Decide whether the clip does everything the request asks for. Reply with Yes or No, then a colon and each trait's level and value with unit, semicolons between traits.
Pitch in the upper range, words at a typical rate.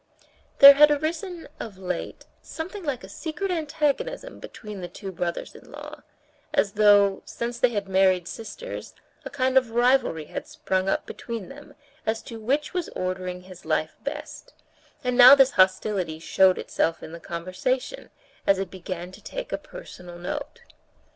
Yes: high, 220 Hz; average, 160 wpm